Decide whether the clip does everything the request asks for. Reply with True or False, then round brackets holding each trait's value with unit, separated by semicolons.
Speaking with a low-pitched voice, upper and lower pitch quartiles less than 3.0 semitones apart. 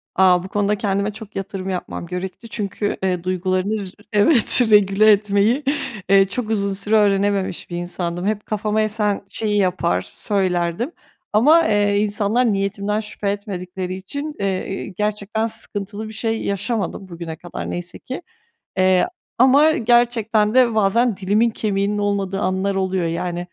False (200 Hz; 2.4 semitones)